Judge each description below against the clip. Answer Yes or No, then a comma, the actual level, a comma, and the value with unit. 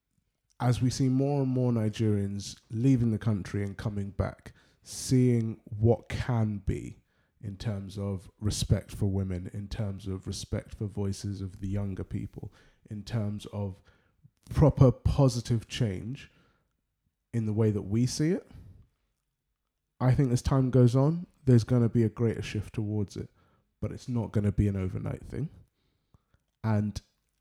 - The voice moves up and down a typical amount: Yes, average, 3.3 semitones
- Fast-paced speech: No, average, 155 wpm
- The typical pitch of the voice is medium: No, low, 110 Hz